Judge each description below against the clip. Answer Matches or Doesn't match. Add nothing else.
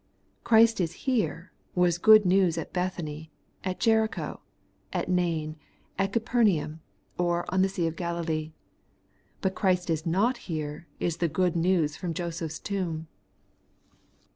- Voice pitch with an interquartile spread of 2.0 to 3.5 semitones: Matches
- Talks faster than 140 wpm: Doesn't match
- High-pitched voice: Doesn't match